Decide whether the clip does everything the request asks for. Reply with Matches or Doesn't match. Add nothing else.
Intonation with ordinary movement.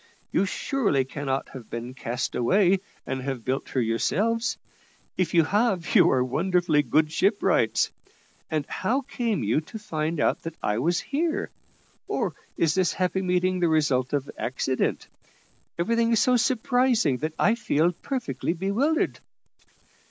Doesn't match